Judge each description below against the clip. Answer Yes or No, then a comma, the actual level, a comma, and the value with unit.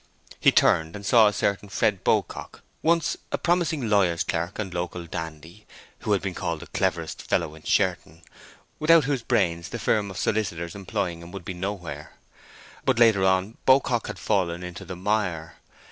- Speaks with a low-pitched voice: Yes, very low, 95 Hz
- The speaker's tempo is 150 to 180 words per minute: Yes, average, 170 wpm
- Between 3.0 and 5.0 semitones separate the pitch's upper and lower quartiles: Yes, average, 4.3 semitones